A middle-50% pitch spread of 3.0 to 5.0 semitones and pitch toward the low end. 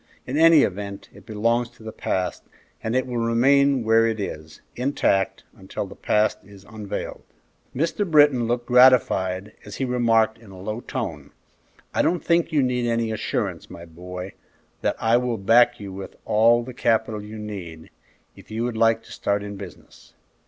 Yes: average, 3.5 semitones; low, 110 Hz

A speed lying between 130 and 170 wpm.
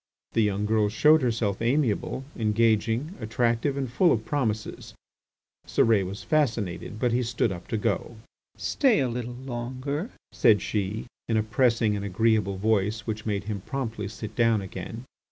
Yes: average, 155 wpm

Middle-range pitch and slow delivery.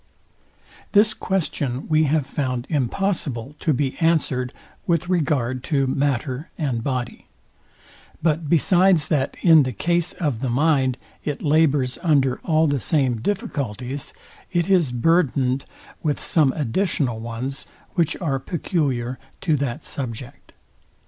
Yes: medium, 145 Hz; slow, 125 wpm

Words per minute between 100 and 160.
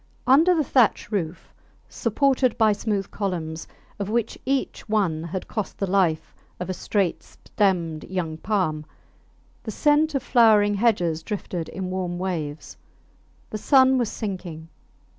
Yes: average, 140 wpm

